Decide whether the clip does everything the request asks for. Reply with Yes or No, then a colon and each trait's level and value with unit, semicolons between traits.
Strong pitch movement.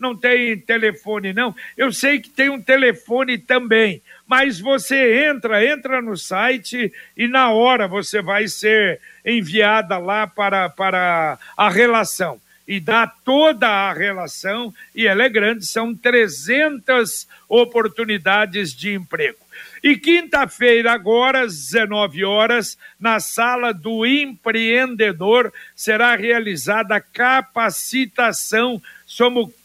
No: average, 3.2 semitones